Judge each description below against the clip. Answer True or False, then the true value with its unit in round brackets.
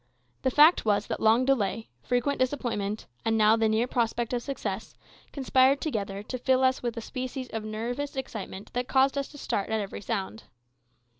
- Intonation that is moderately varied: True (3.4 semitones)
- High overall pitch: True (240 Hz)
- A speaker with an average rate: True (180 wpm)